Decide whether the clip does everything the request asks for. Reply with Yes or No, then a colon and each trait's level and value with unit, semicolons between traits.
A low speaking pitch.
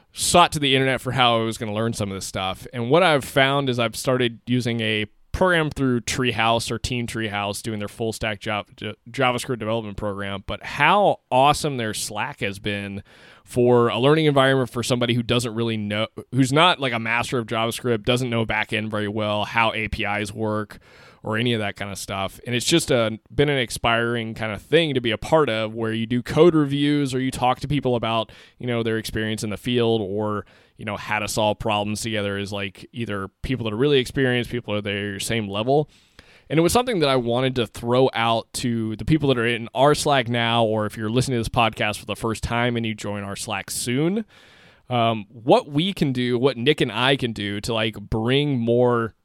Yes: low, 115 Hz